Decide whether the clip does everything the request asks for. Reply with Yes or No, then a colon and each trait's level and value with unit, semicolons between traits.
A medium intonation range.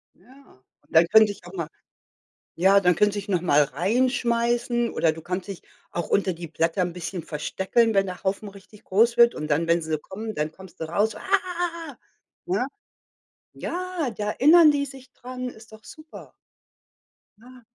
No: wide, 5.8 semitones